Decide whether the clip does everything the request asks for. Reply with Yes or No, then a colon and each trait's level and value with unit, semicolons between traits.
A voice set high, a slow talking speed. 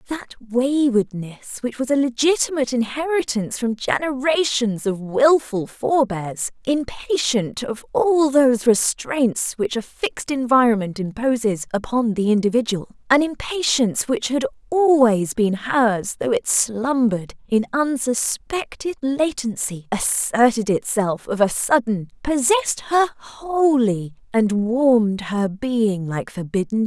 Yes: high, 240 Hz; slow, 120 wpm